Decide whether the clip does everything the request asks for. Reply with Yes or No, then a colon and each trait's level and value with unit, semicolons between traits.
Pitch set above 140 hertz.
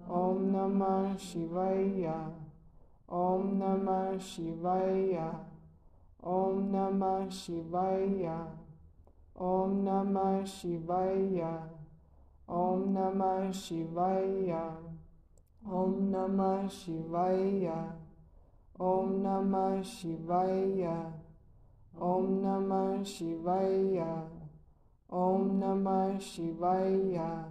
Yes: medium, 185 Hz